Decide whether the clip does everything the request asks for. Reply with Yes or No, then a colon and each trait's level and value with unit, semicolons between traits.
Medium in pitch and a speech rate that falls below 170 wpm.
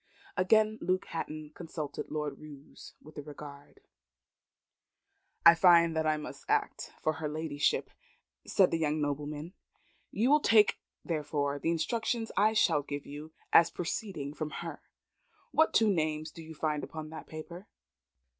Yes: medium, 155 Hz; average, 145 wpm